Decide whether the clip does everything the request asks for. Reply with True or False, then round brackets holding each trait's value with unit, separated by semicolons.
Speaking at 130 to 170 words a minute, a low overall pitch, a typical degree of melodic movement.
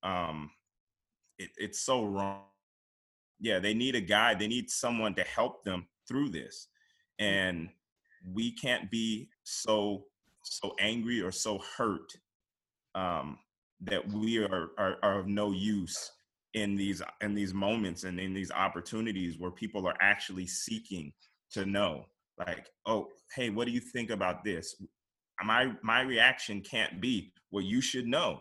True (150 wpm; 100 Hz; 3.0 semitones)